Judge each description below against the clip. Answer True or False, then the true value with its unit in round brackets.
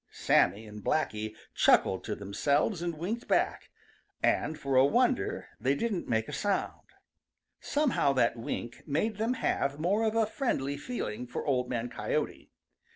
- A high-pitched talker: False (140 Hz)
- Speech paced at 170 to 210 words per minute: False (155 wpm)